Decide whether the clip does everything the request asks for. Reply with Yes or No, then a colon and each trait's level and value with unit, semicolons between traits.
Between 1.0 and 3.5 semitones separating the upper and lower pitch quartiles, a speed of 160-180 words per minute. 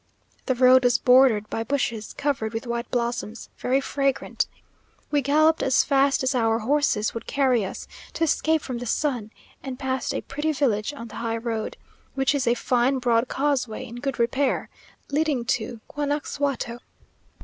Yes: average, 3.1 semitones; average, 165 wpm